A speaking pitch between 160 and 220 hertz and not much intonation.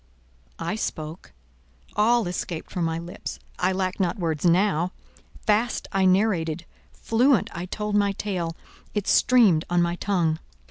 No: medium, 185 Hz; average, 3.6 semitones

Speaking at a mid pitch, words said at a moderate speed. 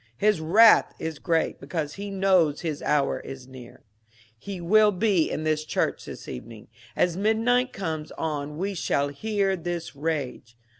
Yes: medium, 165 Hz; average, 155 wpm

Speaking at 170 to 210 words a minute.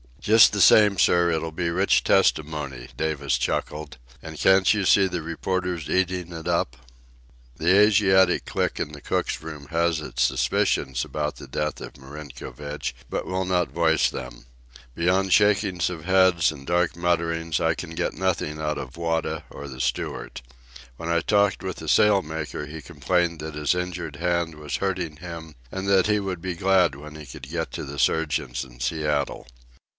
Yes: average, 175 wpm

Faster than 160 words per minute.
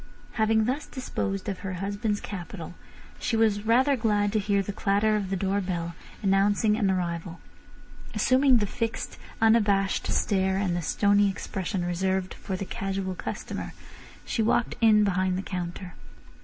No: average, 155 wpm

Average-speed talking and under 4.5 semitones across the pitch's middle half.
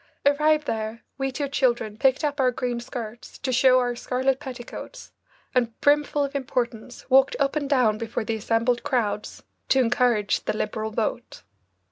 Yes: average, 160 wpm; average, 3.1 semitones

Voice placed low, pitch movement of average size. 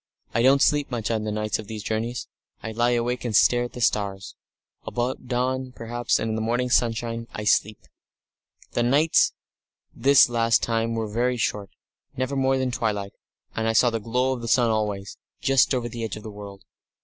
No: low, 115 Hz; narrow, 2.2 semitones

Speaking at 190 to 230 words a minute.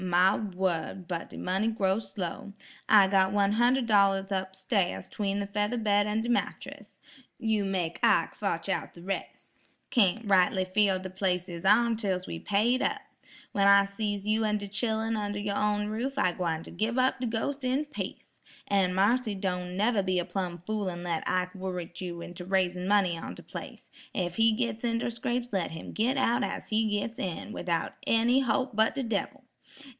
Yes: average, 195 wpm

